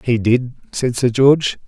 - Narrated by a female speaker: No, male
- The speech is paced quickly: No, average, 180 wpm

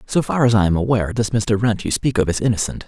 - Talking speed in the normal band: No, fast, 295 wpm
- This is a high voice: No, low, 110 Hz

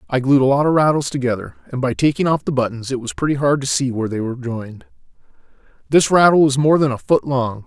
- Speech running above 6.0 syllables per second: Yes, 6.5 syllables/s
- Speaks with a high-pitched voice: No, low, 135 Hz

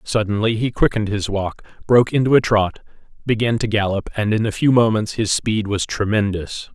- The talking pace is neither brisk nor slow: Yes, average, 185 wpm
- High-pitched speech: No, low, 110 Hz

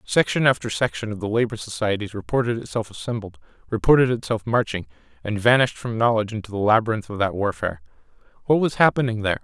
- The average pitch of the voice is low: Yes, low, 110 Hz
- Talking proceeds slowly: No, average, 170 wpm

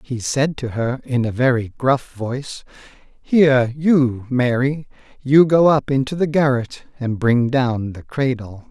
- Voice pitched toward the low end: Yes, low, 130 Hz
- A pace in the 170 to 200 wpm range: No, average, 160 wpm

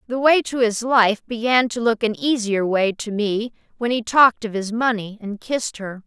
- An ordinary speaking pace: No, fast, 220 wpm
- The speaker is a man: No, female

